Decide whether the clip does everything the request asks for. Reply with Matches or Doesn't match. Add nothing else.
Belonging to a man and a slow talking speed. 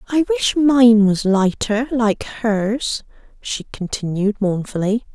Doesn't match